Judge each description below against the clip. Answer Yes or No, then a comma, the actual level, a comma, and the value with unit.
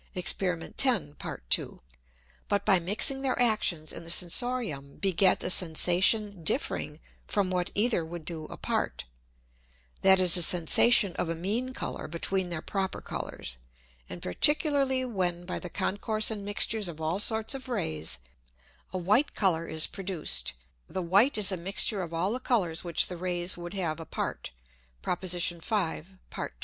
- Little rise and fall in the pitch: No, average, 4.0 semitones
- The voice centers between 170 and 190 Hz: Yes, medium, 185 Hz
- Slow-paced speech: No, average, 160 wpm